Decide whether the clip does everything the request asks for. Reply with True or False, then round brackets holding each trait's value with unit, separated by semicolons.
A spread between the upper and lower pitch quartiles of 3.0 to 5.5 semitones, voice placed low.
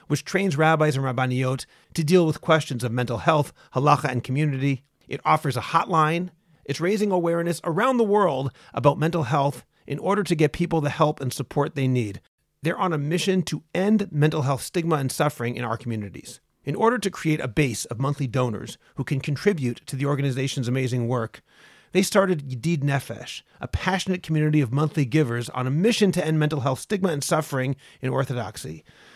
False (4.5 semitones; 150 Hz)